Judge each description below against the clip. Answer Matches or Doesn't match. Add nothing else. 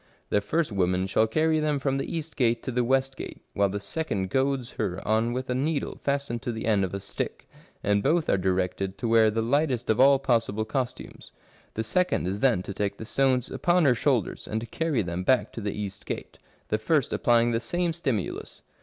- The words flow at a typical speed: Doesn't match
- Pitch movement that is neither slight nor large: Matches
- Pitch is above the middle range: Doesn't match